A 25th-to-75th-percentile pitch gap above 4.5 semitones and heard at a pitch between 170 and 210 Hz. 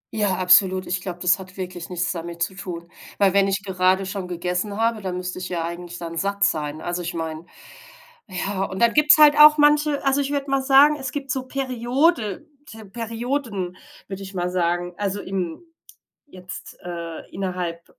Yes: average, 4.9 semitones; high, 190 Hz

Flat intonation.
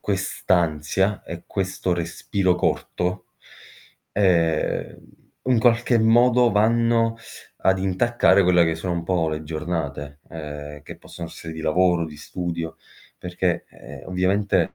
No: average, 3.5 semitones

